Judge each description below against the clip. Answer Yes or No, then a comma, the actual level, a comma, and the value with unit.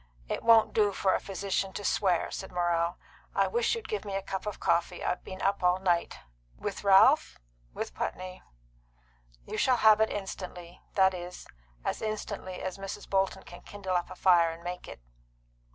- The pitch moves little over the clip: Yes, narrow, 2.3 semitones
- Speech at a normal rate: Yes, average, 185 wpm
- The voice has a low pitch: No, high, 190 Hz